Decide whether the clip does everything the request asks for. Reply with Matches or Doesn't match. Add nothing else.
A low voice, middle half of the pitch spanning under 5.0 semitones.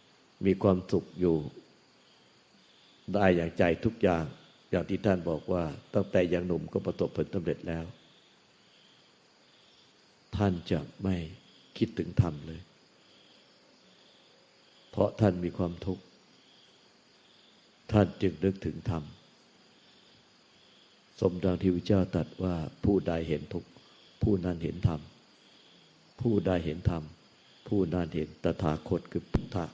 Matches